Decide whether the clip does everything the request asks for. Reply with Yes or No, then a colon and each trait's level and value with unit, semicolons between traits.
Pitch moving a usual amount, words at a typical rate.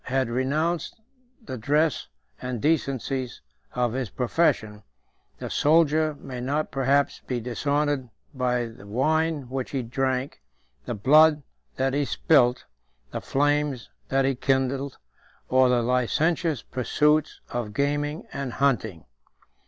No: average, 3.0 semitones; slow, 120 wpm